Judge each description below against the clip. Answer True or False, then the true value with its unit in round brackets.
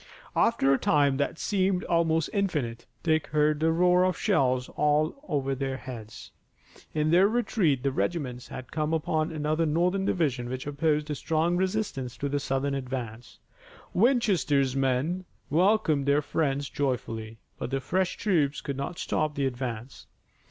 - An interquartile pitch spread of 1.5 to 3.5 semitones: False (4.3 semitones)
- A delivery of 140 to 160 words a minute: True (150 wpm)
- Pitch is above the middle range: False (150 Hz)